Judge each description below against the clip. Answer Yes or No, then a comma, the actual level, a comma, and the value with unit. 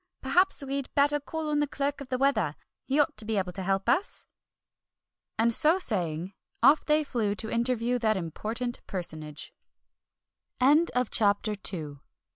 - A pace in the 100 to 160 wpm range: Yes, average, 150 wpm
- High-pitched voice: Yes, high, 235 Hz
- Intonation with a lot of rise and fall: Yes, wide, 6.4 semitones